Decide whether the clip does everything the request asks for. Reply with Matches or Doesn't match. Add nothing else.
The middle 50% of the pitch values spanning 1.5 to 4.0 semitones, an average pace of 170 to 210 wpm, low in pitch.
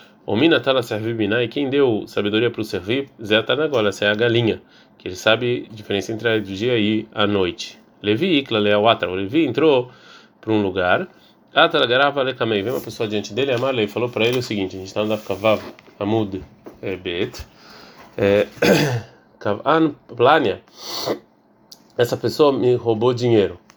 Matches